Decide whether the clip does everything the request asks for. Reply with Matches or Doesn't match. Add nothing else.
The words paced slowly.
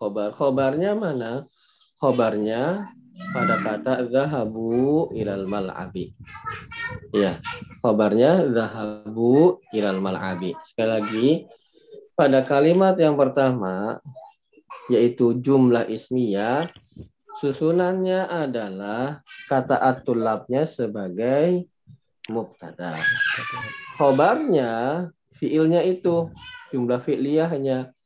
Matches